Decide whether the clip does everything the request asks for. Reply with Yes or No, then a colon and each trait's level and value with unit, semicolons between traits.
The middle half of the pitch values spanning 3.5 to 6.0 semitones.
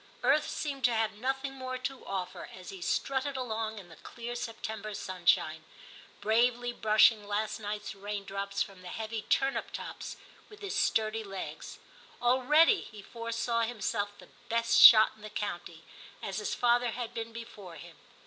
No: average, 3.1 semitones